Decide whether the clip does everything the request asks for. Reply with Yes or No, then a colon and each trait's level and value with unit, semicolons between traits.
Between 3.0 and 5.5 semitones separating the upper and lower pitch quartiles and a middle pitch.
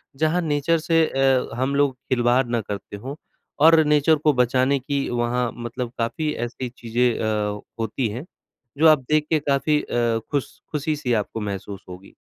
No: average, 4.2 semitones; low, 130 Hz